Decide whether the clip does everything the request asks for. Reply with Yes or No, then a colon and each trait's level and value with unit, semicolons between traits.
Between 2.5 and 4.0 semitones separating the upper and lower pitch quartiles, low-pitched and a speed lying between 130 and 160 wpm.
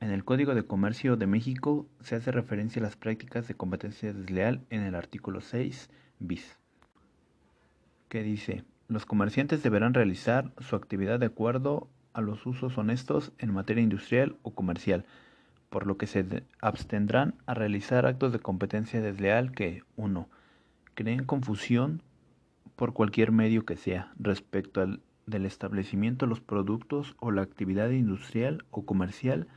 Yes: average, 3.7 semitones; low, 110 Hz; average, 150 wpm